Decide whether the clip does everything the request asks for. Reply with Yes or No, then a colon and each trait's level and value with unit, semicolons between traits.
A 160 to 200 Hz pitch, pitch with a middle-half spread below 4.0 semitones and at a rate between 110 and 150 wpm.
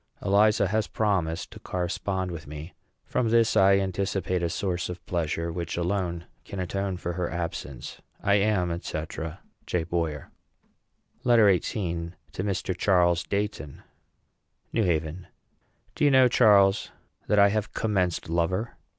No: very low, 90 Hz; average, 3.1 semitones; average, 140 wpm